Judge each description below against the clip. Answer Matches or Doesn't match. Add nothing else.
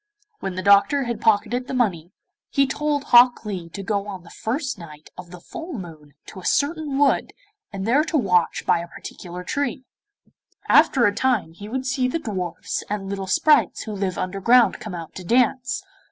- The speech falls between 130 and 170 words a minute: Doesn't match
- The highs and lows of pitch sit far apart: Matches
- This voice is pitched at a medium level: Doesn't match